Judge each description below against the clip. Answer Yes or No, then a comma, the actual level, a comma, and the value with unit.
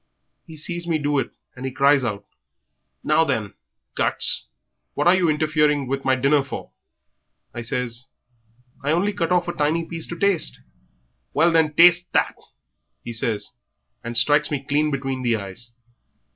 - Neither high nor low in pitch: Yes, medium, 145 Hz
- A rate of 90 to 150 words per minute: No, average, 160 wpm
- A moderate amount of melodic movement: Yes, average, 4.4 semitones